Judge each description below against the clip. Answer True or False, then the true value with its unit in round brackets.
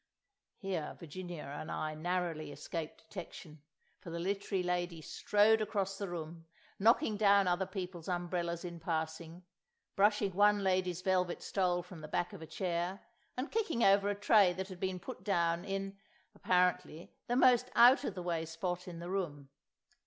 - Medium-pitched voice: True (180 Hz)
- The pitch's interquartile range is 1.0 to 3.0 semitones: True (2.6 semitones)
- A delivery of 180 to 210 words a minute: False (165 wpm)